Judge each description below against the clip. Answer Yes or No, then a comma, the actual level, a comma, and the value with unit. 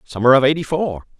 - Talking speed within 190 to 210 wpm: Yes, average, 200 wpm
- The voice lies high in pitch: No, low, 135 Hz